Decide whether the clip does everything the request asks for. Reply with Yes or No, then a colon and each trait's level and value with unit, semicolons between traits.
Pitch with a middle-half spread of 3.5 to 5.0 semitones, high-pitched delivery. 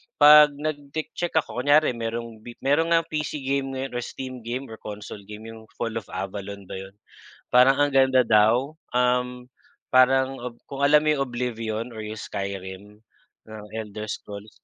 No: average, 4.1 semitones; low, 125 Hz